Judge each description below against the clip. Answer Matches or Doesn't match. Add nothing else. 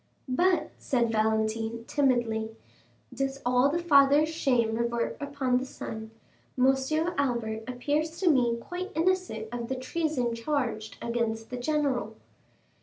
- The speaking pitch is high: Matches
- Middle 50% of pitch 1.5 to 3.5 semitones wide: Doesn't match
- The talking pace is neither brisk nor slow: Doesn't match